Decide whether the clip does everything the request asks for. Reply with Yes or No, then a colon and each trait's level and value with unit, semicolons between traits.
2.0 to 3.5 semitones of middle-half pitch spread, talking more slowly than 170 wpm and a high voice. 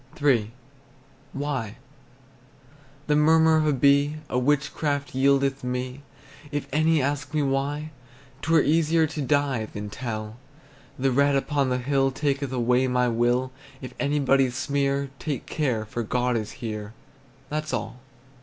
No: average, 2.7 semitones; average, 140 wpm; low, 135 Hz